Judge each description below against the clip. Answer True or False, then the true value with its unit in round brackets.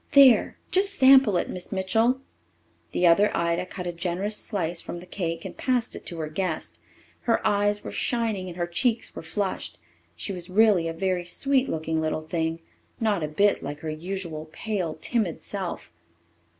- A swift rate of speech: False (175 wpm)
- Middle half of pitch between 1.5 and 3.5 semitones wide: False (4.3 semitones)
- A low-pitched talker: False (185 Hz)